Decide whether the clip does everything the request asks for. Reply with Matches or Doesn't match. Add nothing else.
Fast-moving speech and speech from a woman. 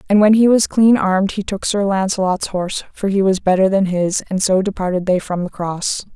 Matches